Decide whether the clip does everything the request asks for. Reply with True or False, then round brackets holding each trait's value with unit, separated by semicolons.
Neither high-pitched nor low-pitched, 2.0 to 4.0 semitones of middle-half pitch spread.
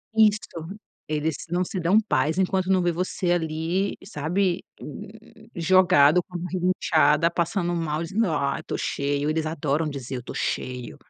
True (170 Hz; 3.3 semitones)